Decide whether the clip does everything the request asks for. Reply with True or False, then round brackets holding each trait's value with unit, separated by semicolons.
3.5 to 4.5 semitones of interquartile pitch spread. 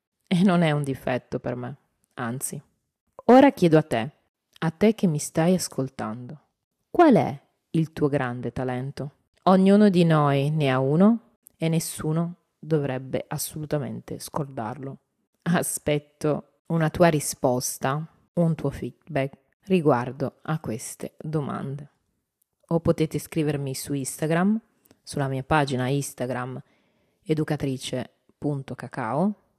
True (4.1 semitones)